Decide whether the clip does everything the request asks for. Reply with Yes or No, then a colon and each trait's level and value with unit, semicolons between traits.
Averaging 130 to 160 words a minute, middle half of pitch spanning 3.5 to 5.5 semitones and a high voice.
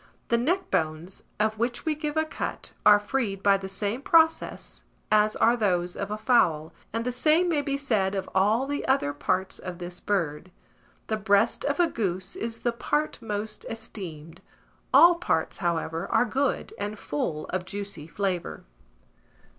No: average, 170 wpm; average, 5.2 semitones; high, 210 Hz